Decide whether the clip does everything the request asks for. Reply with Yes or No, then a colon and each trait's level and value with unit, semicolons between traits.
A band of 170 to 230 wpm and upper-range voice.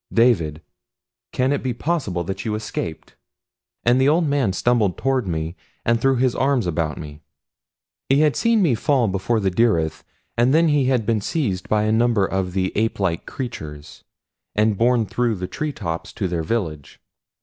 No: average, 175 wpm; low, 115 Hz